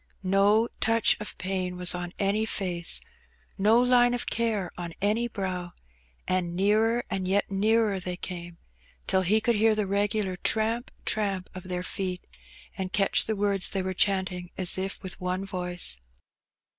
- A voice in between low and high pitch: No, high, 195 Hz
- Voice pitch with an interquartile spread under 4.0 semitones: Yes, average, 2.8 semitones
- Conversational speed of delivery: Yes, average, 160 wpm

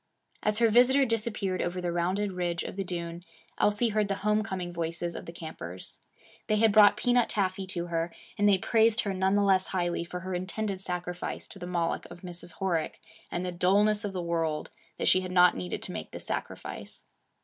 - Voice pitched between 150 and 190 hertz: Yes, medium, 185 Hz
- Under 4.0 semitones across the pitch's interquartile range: Yes, average, 3.0 semitones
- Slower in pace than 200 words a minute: No, fast, 205 wpm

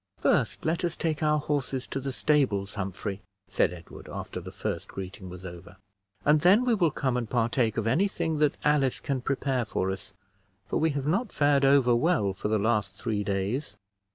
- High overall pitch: No, low, 130 Hz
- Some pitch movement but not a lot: No, wide, 6.8 semitones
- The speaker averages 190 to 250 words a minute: Yes, average, 195 wpm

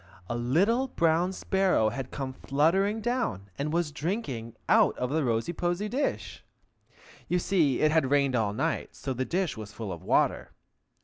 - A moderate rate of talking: Yes, average, 170 wpm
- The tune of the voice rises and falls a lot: Yes, wide, 7.1 semitones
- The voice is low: No, medium, 150 Hz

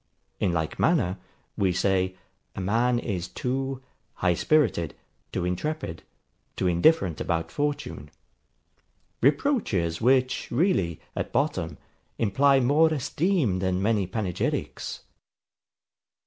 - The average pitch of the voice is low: Yes, low, 110 Hz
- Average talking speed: No, slow, 105 wpm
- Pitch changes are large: Yes, wide, 7.7 semitones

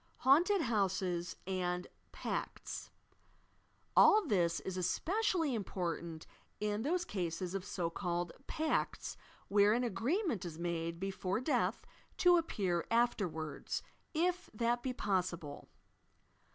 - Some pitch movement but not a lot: No, wide, 6.8 semitones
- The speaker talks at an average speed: No, slow, 110 wpm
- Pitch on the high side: Yes, high, 195 Hz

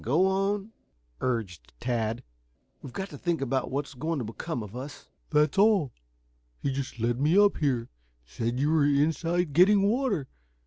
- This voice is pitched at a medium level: Yes, medium, 145 Hz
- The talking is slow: No, average, 165 wpm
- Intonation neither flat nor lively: No, wide, 6.4 semitones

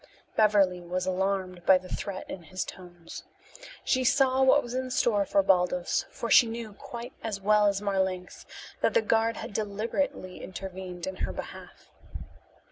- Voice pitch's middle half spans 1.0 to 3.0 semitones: No, average, 3.8 semitones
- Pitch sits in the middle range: No, high, 200 Hz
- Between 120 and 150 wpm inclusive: No, average, 160 wpm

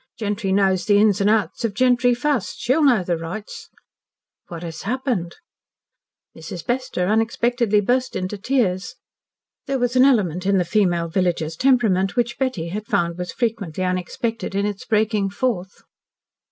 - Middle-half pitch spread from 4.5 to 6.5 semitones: Yes, average, 4.8 semitones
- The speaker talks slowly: No, average, 155 wpm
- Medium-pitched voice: No, high, 205 Hz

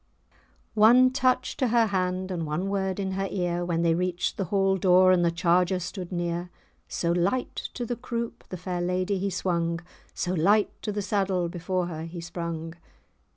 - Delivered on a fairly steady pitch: Yes, narrow, 2.3 semitones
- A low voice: No, medium, 185 Hz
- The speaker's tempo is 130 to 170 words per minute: No, average, 185 wpm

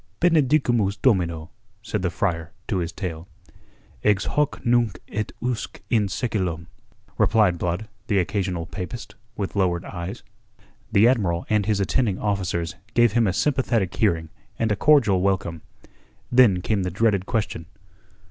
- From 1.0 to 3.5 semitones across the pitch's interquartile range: No, average, 4.4 semitones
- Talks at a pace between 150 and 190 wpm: No, average, 140 wpm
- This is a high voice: No, low, 100 Hz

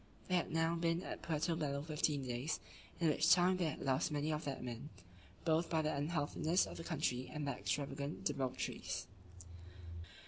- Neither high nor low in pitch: Yes, medium, 155 Hz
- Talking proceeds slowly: No, average, 175 wpm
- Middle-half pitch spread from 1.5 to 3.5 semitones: Yes, average, 2.7 semitones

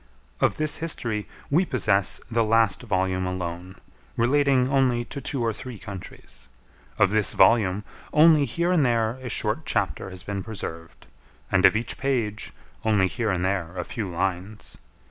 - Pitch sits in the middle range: No, low, 110 Hz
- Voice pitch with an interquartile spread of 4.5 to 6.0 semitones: Yes, average, 5.1 semitones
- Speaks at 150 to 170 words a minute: Yes, average, 160 wpm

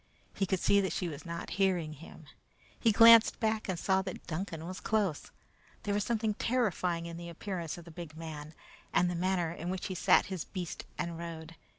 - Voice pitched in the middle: Yes, medium, 175 Hz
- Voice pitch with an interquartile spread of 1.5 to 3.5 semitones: Yes, average, 2.9 semitones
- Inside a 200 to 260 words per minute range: Yes, fast, 205 wpm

